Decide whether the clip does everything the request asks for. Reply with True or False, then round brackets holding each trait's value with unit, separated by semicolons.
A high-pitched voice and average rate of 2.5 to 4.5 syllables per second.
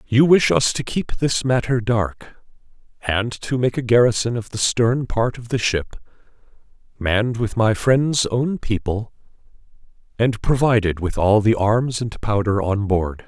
False (115 Hz; 4.2 syllables/s)